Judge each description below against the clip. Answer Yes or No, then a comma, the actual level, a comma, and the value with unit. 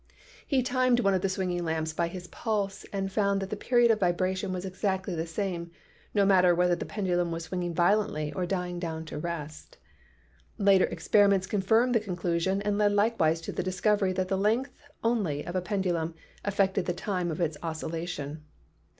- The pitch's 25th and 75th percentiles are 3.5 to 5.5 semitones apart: No, average, 2.9 semitones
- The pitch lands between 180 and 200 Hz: Yes, medium, 185 Hz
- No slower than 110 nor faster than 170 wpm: No, average, 185 wpm